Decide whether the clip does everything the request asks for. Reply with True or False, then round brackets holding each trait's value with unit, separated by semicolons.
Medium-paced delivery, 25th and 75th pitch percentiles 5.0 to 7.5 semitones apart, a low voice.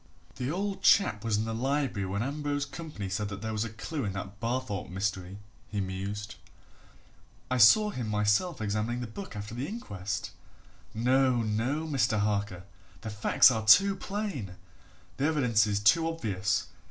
True (160 wpm; 5.4 semitones; 110 Hz)